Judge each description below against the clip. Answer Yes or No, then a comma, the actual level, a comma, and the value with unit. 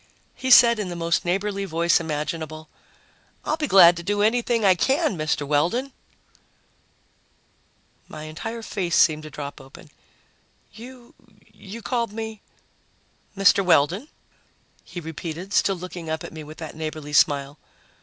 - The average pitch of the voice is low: No, medium, 175 Hz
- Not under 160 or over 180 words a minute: No, average, 145 wpm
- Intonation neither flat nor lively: No, wide, 5.7 semitones